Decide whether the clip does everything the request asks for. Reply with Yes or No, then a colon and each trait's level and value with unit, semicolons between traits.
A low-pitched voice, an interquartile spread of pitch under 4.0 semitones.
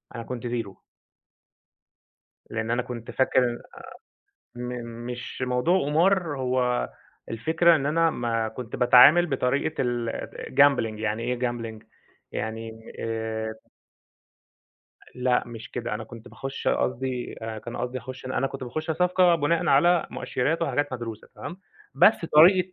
No: low, 125 Hz; average, 4.3 semitones